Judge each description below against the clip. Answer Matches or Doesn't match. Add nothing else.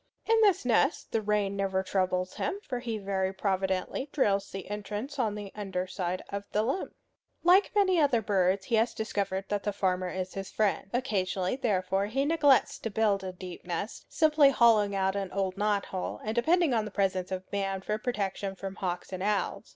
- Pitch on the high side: Matches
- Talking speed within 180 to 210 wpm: Matches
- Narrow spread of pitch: Doesn't match